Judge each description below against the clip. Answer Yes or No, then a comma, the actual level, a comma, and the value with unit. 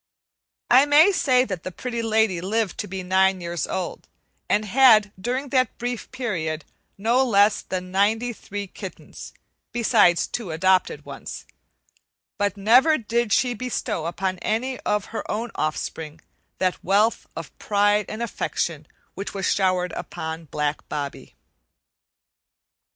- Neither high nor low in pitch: No, high, 205 Hz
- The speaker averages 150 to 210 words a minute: No, slow, 135 wpm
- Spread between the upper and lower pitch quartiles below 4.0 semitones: No, average, 4.5 semitones